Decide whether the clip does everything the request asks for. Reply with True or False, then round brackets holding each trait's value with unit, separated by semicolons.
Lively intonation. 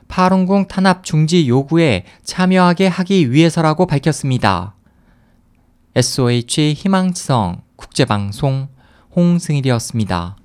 True (8.2 semitones)